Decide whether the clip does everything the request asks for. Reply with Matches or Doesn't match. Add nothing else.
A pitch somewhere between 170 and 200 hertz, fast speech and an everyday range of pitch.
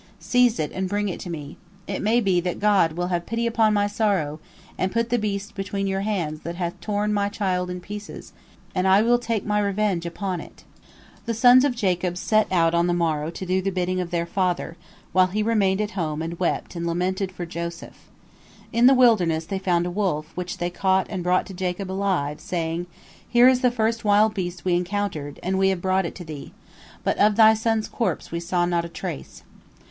Matches